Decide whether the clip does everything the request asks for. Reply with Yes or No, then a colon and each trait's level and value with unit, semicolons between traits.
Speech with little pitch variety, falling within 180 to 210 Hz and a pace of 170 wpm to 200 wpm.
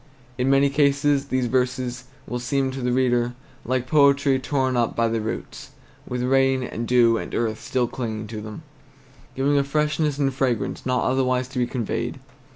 No: narrow, 2.0 semitones; low, 130 Hz; average, 180 wpm